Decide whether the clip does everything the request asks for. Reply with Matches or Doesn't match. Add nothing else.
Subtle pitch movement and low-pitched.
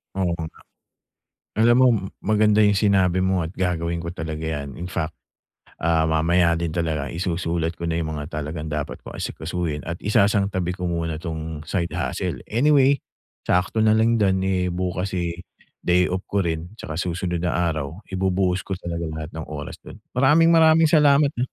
Doesn't match